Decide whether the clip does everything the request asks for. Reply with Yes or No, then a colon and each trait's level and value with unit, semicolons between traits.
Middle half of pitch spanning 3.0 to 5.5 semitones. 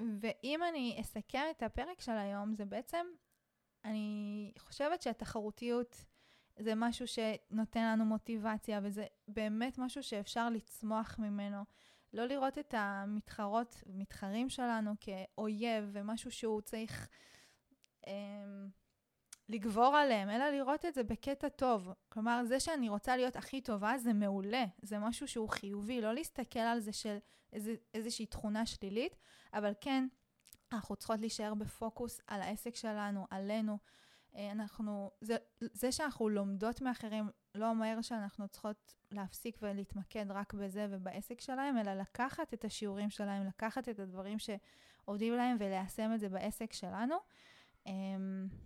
No: narrow, 2.6 semitones